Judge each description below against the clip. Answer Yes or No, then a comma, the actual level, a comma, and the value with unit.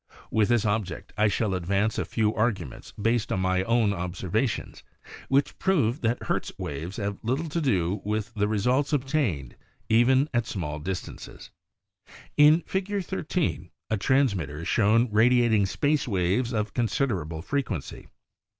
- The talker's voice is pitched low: Yes, low, 110 Hz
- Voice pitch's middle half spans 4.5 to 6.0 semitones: Yes, average, 5.1 semitones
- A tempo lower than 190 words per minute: Yes, average, 150 wpm